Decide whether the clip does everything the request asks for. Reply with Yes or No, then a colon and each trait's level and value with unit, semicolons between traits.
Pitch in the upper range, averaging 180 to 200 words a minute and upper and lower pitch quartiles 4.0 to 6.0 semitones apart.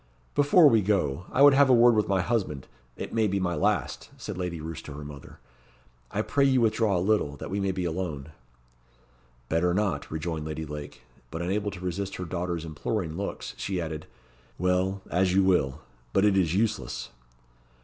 No: very low, 90 Hz; average, 190 wpm; average, 4.5 semitones